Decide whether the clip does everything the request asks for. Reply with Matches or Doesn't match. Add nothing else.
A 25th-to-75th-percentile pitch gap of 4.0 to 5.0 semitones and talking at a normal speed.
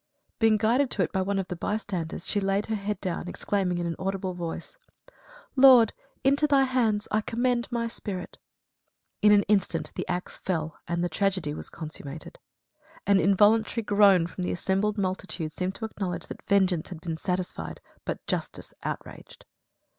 Doesn't match